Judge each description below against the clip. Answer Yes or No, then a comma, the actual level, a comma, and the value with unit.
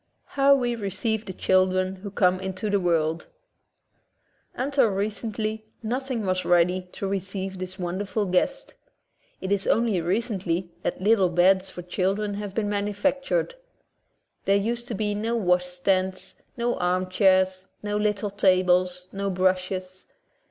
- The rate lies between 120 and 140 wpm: Yes, slow, 135 wpm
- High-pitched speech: Yes, high, 195 Hz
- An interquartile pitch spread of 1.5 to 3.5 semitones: Yes, narrow, 2.5 semitones